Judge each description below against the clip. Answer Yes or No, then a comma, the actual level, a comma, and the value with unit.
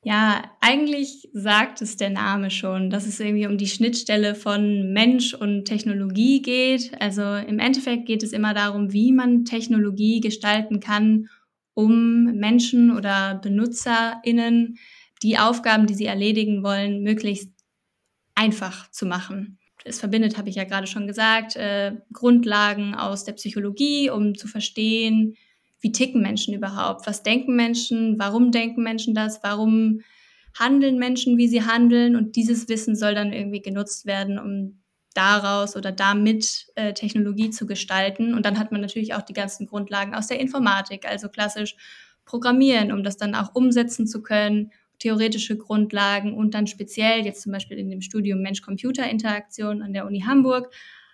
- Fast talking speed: No, average, 155 wpm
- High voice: Yes, high, 215 Hz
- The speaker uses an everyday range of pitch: No, narrow, 2.2 semitones